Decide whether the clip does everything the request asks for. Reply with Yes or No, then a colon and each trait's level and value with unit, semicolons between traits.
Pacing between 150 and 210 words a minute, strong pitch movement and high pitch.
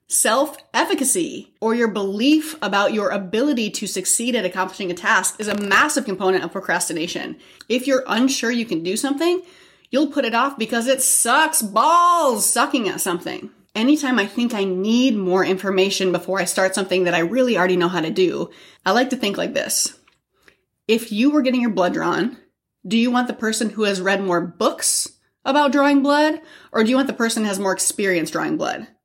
Yes: average, 195 wpm; wide, 6.0 semitones; high, 225 Hz